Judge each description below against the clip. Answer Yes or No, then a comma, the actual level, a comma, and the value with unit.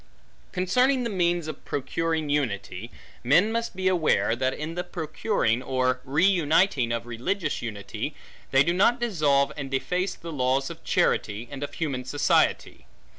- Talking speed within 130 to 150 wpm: Yes, average, 145 wpm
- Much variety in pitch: Yes, wide, 5.9 semitones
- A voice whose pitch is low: No, medium, 150 Hz